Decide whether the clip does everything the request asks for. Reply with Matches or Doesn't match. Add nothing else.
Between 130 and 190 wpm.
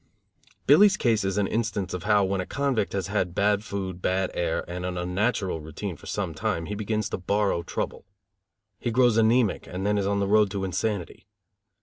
Doesn't match